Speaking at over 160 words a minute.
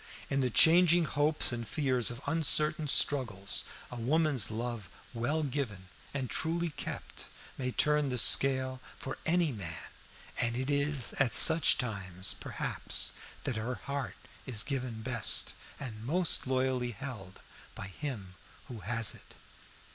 No: average, 140 wpm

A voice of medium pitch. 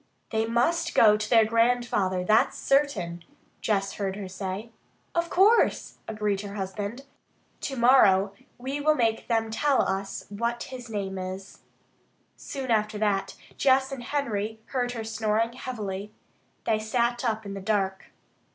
No: high, 220 Hz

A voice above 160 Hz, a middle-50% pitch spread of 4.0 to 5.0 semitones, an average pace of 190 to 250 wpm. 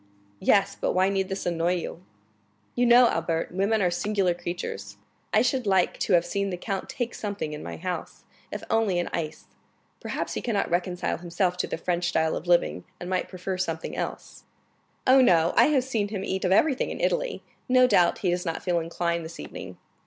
No: medium, 185 Hz; average, 2.9 semitones; average, 200 wpm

